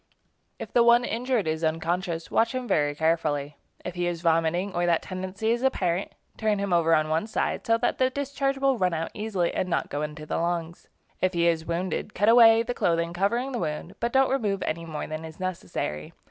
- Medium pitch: Yes, medium, 180 Hz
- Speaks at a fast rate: Yes, fast, 215 wpm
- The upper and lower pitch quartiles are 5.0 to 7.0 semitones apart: Yes, wide, 5.6 semitones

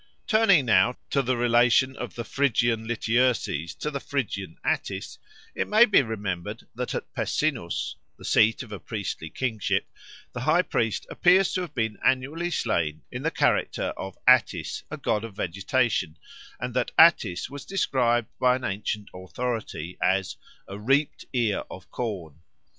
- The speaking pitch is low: Yes, low, 120 Hz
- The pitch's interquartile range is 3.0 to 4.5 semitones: No, average, 4.9 semitones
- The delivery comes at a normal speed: Yes, average, 155 wpm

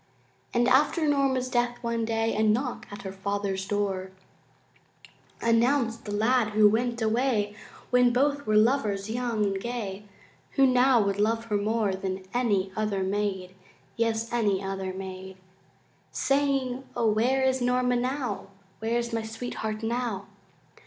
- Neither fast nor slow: Yes, average, 145 wpm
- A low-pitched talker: No, high, 225 Hz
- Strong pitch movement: No, average, 3.4 semitones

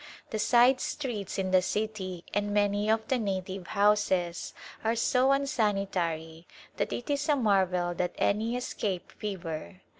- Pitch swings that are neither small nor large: Yes, average, 3.5 semitones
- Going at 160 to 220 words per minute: No, average, 145 wpm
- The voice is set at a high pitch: Yes, high, 205 Hz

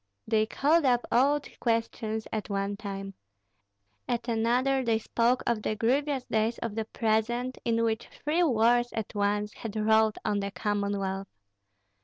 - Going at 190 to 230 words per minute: No, average, 150 wpm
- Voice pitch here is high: Yes, high, 225 Hz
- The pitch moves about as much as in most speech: No, narrow, 2.3 semitones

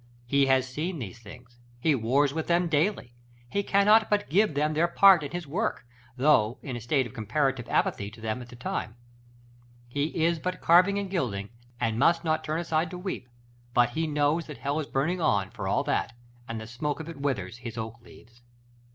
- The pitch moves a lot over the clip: Yes, wide, 5.8 semitones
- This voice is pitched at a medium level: Yes, medium, 145 Hz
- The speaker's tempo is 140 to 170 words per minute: No, fast, 205 wpm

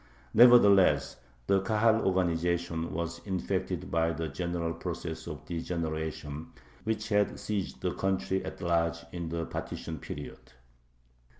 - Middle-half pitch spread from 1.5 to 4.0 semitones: Yes, average, 2.8 semitones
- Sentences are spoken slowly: Yes, slow, 120 wpm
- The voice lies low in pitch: Yes, very low, 85 Hz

